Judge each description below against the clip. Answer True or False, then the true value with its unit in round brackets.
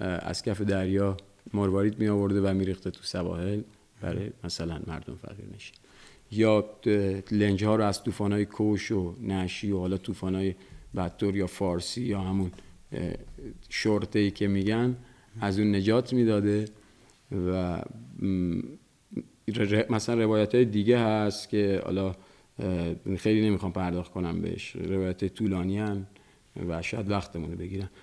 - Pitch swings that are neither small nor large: False (2.2 semitones)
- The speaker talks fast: False (130 wpm)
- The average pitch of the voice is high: False (100 Hz)